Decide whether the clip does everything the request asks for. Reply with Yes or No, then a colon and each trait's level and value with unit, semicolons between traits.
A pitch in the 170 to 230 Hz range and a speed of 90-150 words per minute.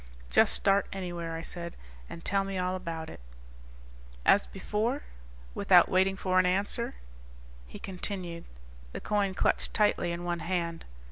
Yes: medium, 185 Hz; average, 145 wpm